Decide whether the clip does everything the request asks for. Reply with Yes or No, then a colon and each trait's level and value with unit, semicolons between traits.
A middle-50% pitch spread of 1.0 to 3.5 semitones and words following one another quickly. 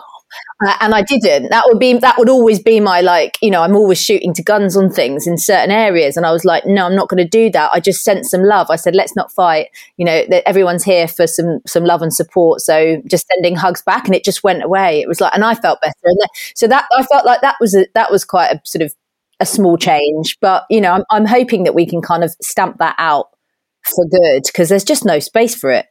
No: average, 4.2 semitones; fast, 265 wpm